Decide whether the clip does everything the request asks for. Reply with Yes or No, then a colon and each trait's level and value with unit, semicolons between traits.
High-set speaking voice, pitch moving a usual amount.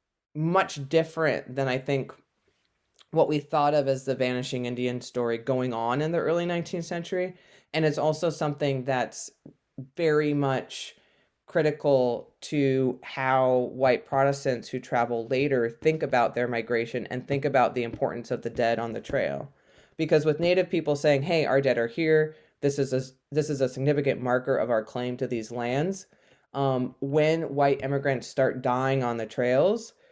No: low, 135 Hz; average, 3.5 semitones